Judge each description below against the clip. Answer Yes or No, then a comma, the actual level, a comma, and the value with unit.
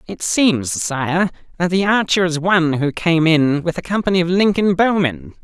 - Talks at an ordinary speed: Yes, average, 190 wpm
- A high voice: No, medium, 170 Hz